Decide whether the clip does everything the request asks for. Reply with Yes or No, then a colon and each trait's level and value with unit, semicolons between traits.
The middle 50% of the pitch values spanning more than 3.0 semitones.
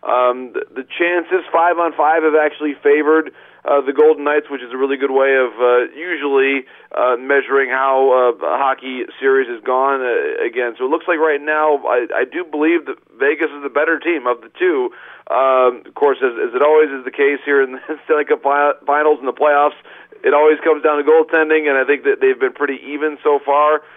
Yes: average, 3.9 semitones